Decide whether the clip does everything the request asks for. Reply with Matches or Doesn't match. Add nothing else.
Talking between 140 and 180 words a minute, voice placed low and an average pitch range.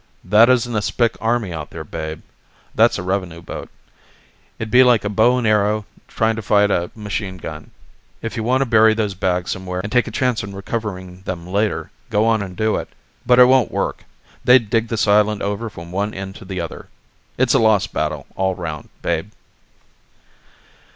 Doesn't match